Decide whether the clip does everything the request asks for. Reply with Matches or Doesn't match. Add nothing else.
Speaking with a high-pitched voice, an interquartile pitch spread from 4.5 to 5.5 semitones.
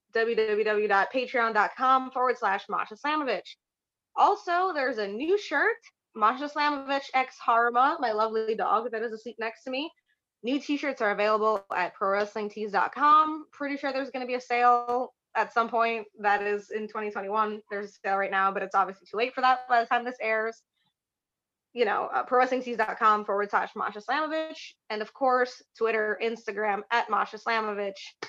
Doesn't match